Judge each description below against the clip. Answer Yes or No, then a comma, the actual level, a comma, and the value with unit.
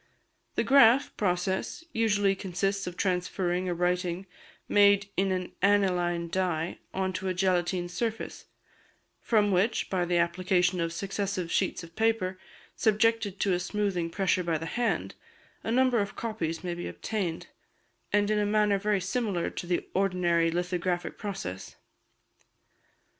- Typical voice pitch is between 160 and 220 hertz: Yes, medium, 185 Hz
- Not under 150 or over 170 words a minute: No, average, 140 wpm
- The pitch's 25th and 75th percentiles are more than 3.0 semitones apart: No, narrow, 2.5 semitones